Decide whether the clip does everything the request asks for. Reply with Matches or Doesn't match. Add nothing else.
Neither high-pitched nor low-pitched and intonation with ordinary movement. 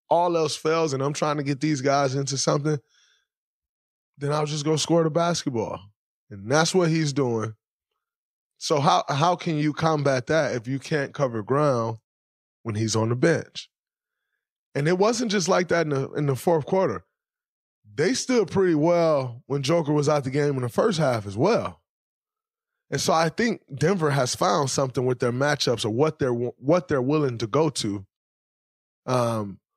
Matches